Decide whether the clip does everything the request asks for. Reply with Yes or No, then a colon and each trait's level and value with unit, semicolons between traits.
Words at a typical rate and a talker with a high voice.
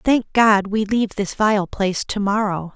Yes: average, 175 wpm; high, 205 Hz